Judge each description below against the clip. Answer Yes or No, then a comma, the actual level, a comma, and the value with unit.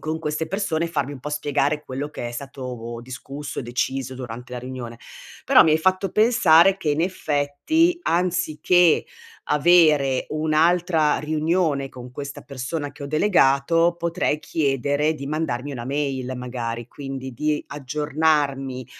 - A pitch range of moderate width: Yes, average, 3.5 semitones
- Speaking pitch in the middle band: Yes, medium, 145 Hz